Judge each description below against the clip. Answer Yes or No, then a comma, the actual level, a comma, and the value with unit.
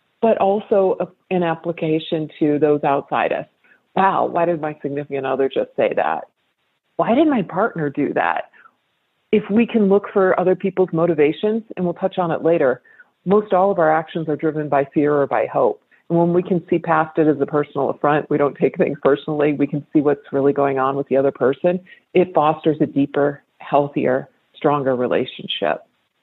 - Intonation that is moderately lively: Yes, average, 3.9 semitones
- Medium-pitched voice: Yes, medium, 160 Hz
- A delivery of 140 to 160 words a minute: No, average, 190 wpm